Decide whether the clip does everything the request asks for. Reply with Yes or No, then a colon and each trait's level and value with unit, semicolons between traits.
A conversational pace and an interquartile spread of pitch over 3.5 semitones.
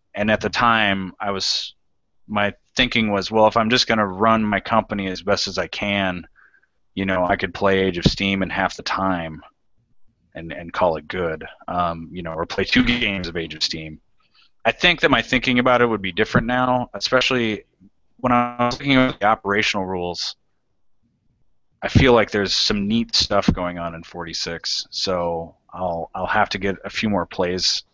Yes: average, 195 wpm; average, 3.9 semitones